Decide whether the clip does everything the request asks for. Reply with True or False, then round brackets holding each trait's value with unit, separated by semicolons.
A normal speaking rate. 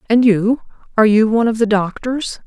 True (195 wpm)